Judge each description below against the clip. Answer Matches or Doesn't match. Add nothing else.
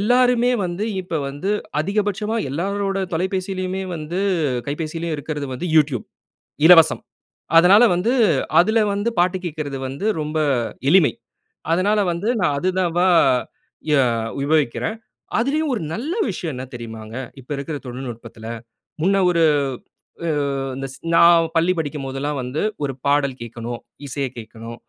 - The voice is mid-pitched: Matches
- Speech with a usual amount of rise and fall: Doesn't match